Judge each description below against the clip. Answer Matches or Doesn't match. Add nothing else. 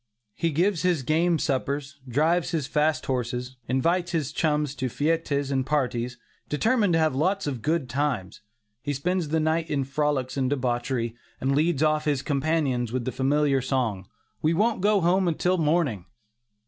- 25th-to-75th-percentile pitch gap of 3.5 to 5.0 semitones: Matches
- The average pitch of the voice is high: Doesn't match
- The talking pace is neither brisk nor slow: Matches